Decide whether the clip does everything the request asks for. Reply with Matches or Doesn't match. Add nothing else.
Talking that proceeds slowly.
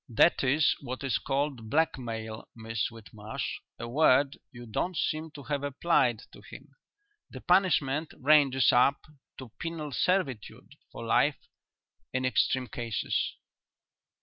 Matches